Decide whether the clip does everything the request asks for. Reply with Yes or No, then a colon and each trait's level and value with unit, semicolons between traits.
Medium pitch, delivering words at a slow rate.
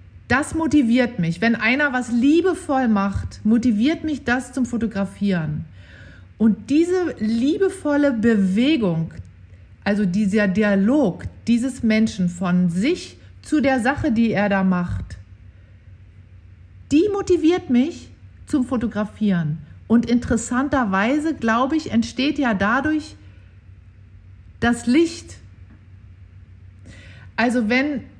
No: high, 225 Hz; slow, 100 wpm